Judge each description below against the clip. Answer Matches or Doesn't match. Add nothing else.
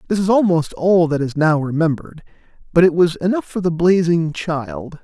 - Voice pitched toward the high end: Doesn't match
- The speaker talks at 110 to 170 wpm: Doesn't match